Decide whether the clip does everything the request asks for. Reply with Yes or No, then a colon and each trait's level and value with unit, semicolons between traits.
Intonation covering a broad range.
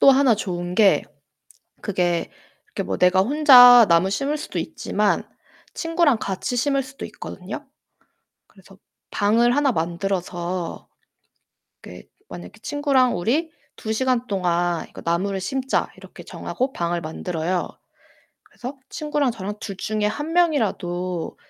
Yes: wide, 7.0 semitones